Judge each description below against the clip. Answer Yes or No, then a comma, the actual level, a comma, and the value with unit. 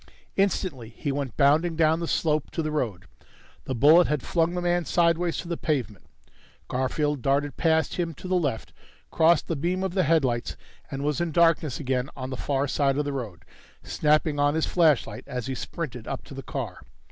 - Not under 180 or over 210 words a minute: Yes, average, 195 wpm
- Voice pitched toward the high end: No, medium, 150 Hz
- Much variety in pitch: No, average, 3.9 semitones